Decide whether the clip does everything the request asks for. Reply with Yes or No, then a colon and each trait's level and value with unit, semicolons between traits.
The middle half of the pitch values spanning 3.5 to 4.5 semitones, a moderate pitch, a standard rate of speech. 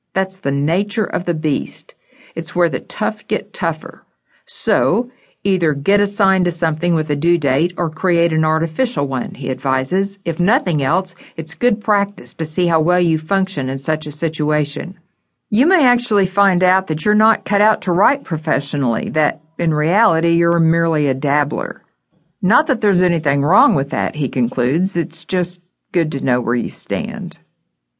Yes: average, 4.1 semitones; medium, 170 Hz; average, 175 wpm